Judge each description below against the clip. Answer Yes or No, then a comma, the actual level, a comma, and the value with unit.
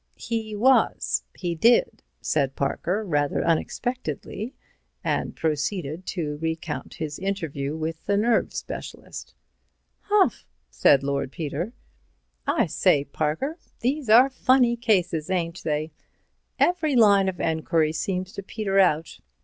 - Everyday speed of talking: No, slow, 120 wpm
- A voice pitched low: No, medium, 180 Hz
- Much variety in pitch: Yes, wide, 6.4 semitones